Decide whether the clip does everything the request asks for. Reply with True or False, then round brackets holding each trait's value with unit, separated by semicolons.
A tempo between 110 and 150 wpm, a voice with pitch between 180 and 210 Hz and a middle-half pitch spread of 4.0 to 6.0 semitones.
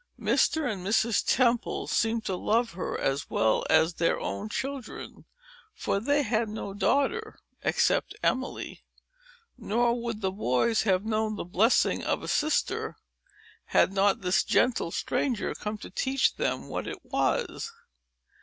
False (145 wpm; 220 Hz; 4.3 semitones)